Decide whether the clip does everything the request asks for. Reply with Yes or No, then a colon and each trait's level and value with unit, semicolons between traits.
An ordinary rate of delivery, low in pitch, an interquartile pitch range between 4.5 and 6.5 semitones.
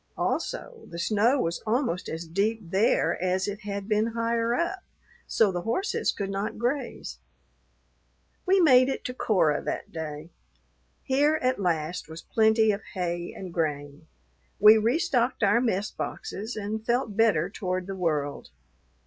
No: average, 150 wpm; high, 210 Hz; average, 4.9 semitones